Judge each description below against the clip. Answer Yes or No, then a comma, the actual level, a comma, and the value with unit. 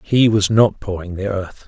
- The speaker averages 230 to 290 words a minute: No, fast, 215 wpm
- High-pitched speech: No, low, 100 Hz